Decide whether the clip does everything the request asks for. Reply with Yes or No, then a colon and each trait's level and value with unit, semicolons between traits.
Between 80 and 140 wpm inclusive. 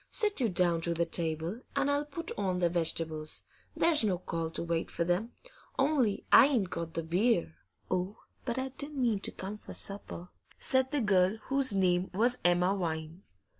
No: average, 185 wpm